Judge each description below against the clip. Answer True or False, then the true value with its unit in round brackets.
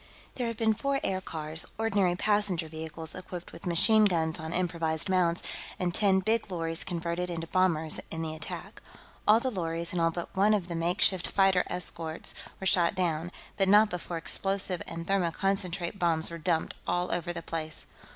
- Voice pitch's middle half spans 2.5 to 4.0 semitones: True (2.8 semitones)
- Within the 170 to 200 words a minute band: True (175 wpm)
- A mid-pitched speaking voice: True (175 Hz)